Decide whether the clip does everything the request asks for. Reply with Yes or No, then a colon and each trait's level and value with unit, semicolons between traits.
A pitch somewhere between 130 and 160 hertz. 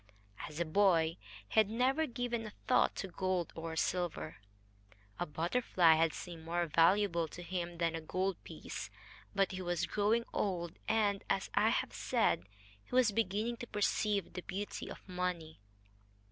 No: medium, 185 Hz